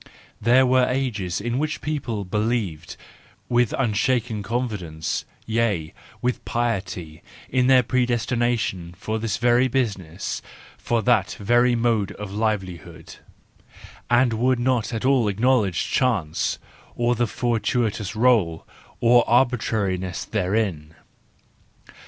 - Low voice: Yes, low, 115 Hz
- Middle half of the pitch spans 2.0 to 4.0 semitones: Yes, average, 3.7 semitones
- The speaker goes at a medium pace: No, slow, 110 wpm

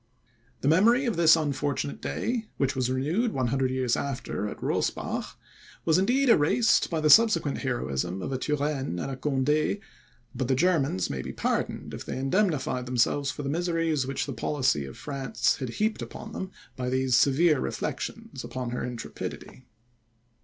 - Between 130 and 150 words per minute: No, average, 160 wpm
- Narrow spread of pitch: No, average, 4.4 semitones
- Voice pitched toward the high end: No, medium, 140 Hz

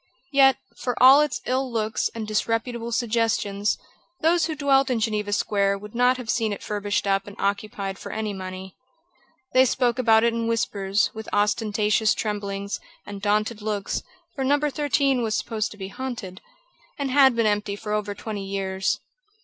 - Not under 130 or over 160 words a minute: No, average, 170 wpm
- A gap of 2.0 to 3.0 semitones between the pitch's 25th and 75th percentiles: No, average, 3.5 semitones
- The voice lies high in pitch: Yes, high, 220 Hz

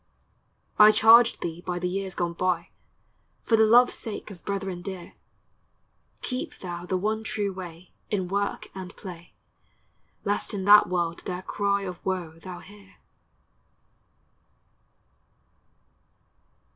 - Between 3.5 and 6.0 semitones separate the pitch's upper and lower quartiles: No, narrow, 2.6 semitones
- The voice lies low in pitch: No, high, 190 Hz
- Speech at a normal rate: No, slow, 125 wpm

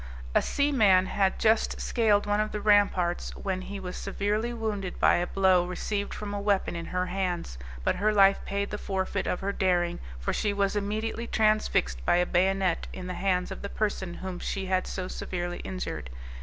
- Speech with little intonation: Yes, narrow, 2.2 semitones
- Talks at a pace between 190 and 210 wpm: Yes, average, 195 wpm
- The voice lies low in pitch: No, high, 195 Hz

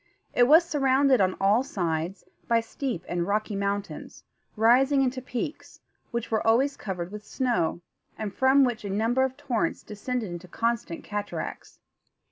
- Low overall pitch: No, high, 230 Hz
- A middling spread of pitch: Yes, average, 4.6 semitones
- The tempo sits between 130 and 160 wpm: Yes, average, 150 wpm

